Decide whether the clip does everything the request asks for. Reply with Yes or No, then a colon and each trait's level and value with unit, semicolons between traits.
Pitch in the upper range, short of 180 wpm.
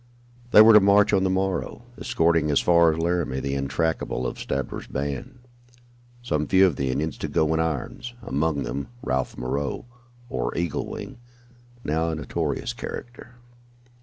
No: very low, 80 Hz; average, 160 wpm